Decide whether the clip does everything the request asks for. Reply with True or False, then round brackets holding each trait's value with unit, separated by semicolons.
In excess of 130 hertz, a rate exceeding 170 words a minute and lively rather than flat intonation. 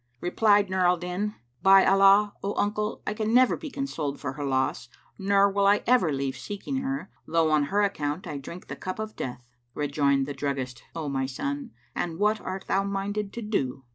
True (190 Hz; 200 wpm; 6.4 semitones)